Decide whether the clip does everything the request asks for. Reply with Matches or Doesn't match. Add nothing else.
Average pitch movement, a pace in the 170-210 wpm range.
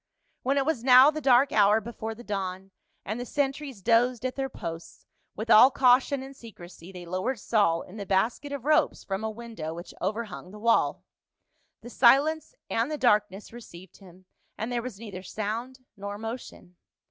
Matches